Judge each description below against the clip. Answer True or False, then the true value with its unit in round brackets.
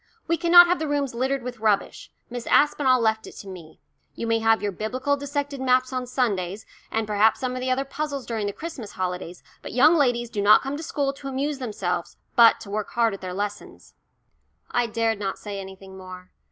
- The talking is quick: True (210 wpm)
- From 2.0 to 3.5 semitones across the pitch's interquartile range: False (5.0 semitones)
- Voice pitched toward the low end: False (235 Hz)